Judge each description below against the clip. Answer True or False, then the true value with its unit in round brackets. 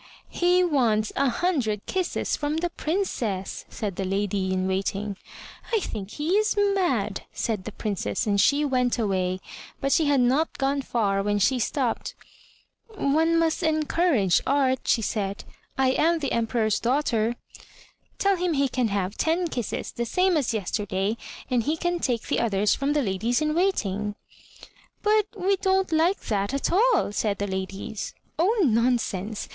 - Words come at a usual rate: True (160 wpm)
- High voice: True (250 Hz)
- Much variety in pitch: True (7.7 semitones)